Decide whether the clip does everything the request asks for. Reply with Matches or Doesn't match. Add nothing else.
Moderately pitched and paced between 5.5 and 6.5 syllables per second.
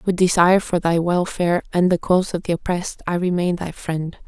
Matches